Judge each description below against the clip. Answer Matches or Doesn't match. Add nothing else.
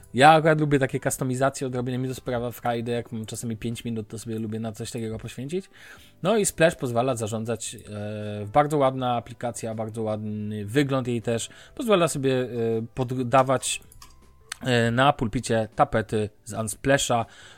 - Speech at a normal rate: Matches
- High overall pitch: Doesn't match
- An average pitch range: Matches